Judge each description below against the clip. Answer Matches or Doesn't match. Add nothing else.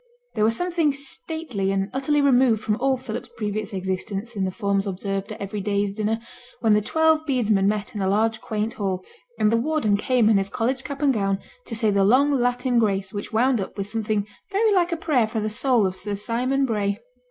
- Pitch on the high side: Matches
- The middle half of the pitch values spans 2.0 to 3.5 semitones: Doesn't match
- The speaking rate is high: Matches